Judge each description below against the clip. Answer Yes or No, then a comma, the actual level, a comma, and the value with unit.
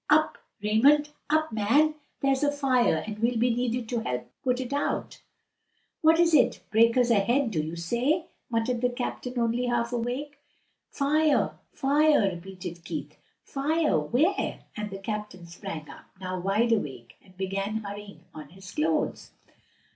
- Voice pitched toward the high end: Yes, high, 235 Hz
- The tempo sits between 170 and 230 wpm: No, average, 150 wpm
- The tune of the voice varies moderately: No, wide, 6.0 semitones